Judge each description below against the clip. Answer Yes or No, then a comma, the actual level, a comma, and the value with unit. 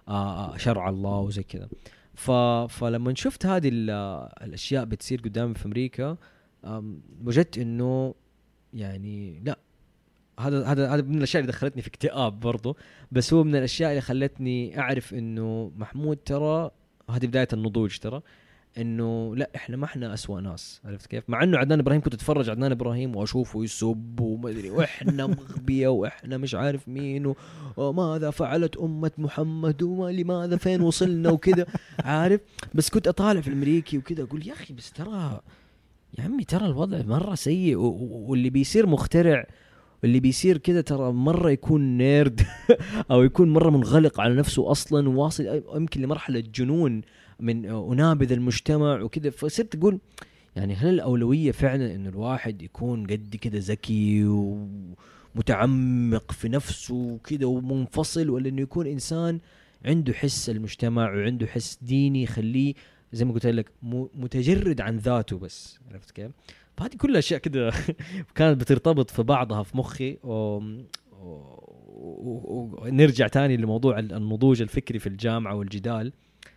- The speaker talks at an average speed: No, fast, 140 wpm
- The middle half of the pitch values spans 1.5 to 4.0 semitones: No, average, 5.0 semitones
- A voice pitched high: No, low, 130 Hz